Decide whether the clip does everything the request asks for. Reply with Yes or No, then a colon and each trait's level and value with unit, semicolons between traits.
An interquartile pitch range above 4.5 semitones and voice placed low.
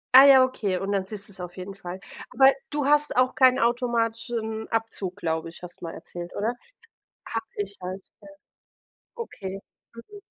No: average, 5.1 semitones; high, 220 Hz